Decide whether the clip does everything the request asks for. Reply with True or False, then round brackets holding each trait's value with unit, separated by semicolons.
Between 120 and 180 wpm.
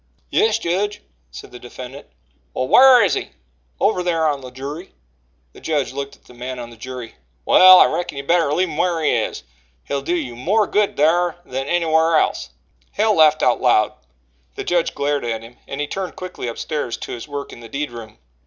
False (205 wpm)